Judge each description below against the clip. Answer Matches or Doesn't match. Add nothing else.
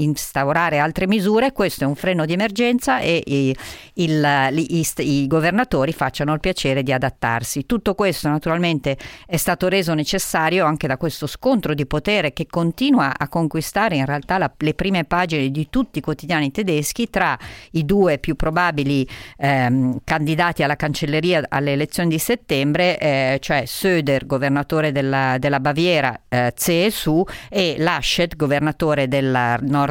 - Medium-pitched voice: Matches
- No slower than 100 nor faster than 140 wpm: Doesn't match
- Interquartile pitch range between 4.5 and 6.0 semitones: Doesn't match